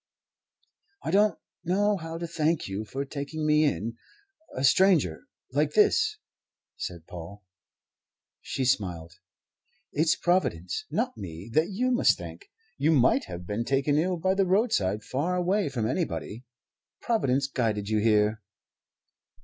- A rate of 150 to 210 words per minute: No, slow, 135 wpm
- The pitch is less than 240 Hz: Yes, medium, 140 Hz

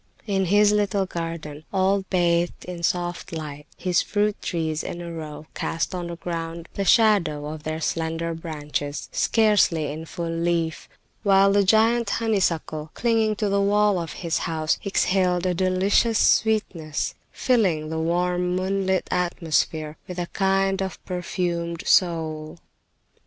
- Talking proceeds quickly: No, average, 140 wpm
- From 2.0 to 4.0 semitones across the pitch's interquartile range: Yes, average, 3.2 semitones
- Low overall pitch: No, medium, 175 Hz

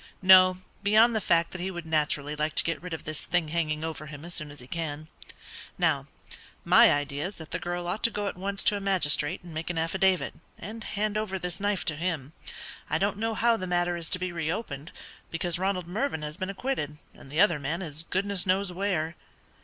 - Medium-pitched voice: Yes, medium, 175 Hz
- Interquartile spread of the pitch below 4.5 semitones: Yes, average, 3.8 semitones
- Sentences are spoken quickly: Yes, fast, 225 wpm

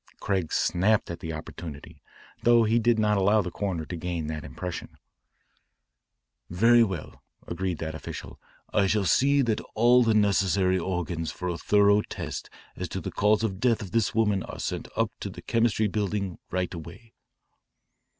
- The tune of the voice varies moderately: Yes, average, 3.8 semitones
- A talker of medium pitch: No, low, 100 Hz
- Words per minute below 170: No, average, 175 wpm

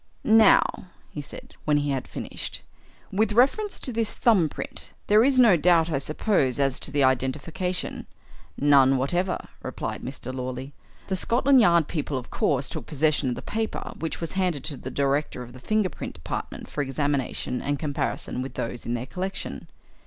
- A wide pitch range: Yes, wide, 6.1 semitones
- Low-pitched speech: No, medium, 150 Hz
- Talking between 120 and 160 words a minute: No, average, 175 wpm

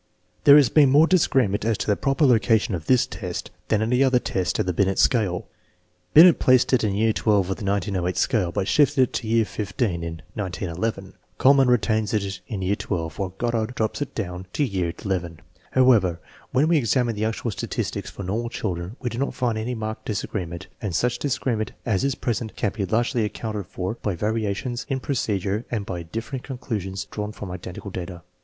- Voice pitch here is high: No, low, 110 Hz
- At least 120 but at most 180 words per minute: No, average, 200 wpm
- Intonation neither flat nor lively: Yes, average, 4.3 semitones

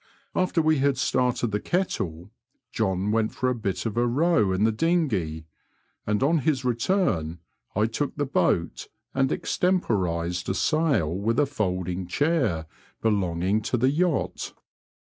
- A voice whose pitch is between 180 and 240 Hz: No, low, 115 Hz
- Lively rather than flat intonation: Yes, wide, 7.6 semitones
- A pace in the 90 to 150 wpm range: Yes, average, 145 wpm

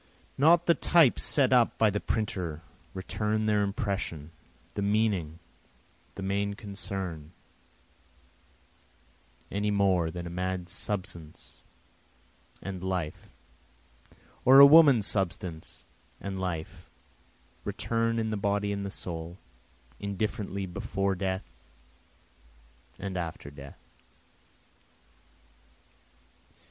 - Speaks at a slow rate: Yes, slow, 95 wpm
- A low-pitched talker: Yes, low, 100 Hz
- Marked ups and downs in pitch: No, average, 3.1 semitones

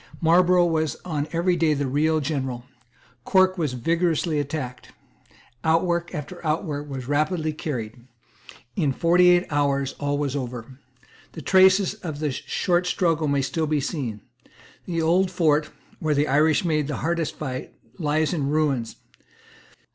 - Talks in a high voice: No, medium, 155 Hz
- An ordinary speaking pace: Yes, average, 145 wpm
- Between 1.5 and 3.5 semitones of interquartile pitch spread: Yes, average, 3.2 semitones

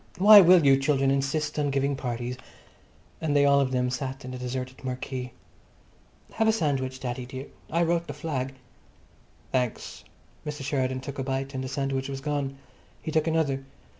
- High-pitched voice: No, low, 135 Hz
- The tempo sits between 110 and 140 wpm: No, average, 180 wpm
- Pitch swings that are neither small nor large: No, narrow, 2.3 semitones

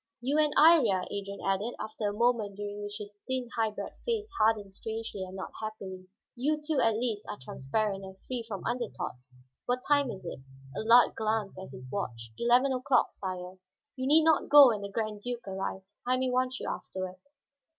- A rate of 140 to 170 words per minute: No, average, 190 wpm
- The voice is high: Yes, high, 215 Hz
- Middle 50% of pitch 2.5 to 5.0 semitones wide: Yes, average, 4.5 semitones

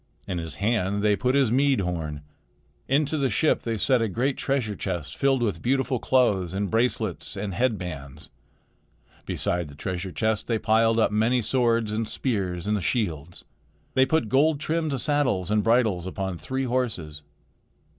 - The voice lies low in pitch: Yes, low, 110 Hz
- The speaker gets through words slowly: No, average, 165 wpm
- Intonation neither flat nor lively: No, wide, 5.7 semitones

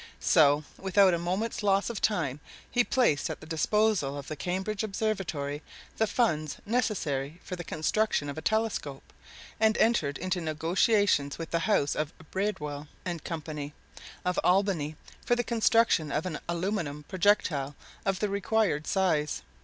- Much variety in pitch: Yes, wide, 5.8 semitones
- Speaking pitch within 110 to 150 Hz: No, medium, 180 Hz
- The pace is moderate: Yes, average, 150 wpm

